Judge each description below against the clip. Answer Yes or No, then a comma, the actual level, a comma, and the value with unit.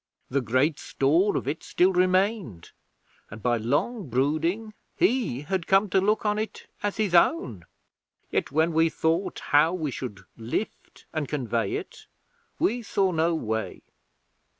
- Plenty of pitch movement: Yes, wide, 7.0 semitones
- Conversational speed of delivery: Yes, average, 150 wpm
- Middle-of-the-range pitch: Yes, medium, 160 Hz